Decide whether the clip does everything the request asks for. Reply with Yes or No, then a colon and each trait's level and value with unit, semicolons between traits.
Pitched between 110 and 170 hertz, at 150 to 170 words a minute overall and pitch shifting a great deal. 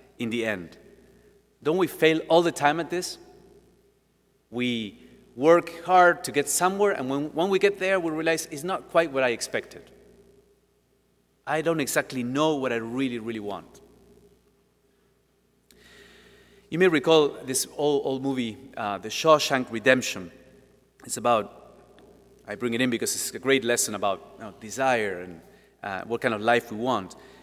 Yes: low, 135 Hz; average, 160 wpm; wide, 5.9 semitones